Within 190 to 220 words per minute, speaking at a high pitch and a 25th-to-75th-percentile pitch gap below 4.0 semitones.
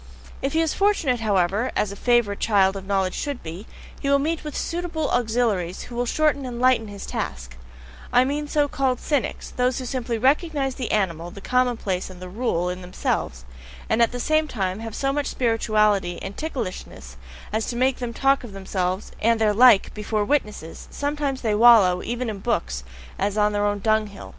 No: average, 195 wpm; high, 225 Hz; average, 5.1 semitones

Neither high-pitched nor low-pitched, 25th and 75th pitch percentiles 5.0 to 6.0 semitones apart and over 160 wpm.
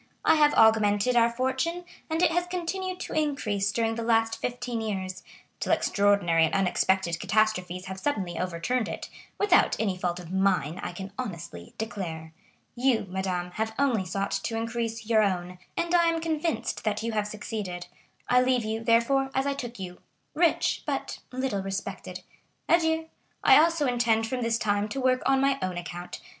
No: high, 225 Hz; wide, 5.6 semitones; average, 170 wpm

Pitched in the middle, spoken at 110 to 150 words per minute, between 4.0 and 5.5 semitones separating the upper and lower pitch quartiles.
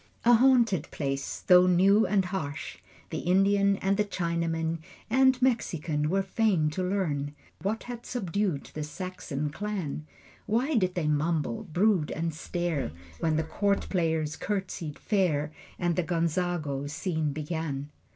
Yes: medium, 175 Hz; average, 140 wpm; average, 4.5 semitones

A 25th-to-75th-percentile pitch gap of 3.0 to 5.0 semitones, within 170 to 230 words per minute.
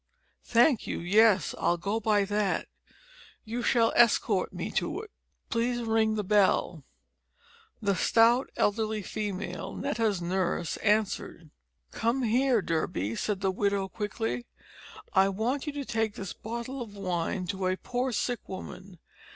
No: average, 3.5 semitones; average, 140 wpm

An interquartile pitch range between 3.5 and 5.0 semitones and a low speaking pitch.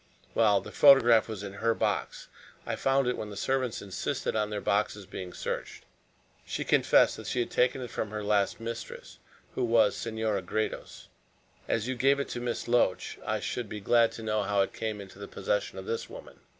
No: average, 3.1 semitones; low, 110 Hz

